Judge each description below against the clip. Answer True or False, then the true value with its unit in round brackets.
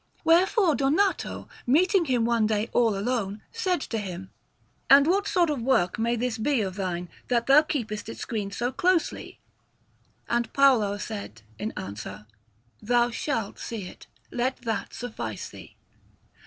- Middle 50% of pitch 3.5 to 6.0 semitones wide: True (5.2 semitones)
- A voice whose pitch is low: False (235 Hz)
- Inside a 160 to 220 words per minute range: False (150 wpm)